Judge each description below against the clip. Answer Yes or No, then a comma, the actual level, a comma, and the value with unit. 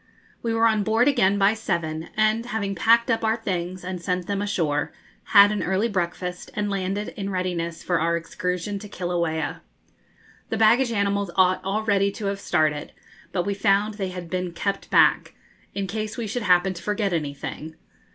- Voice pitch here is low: No, high, 195 Hz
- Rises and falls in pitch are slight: No, average, 3.2 semitones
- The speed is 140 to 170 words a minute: No, average, 180 wpm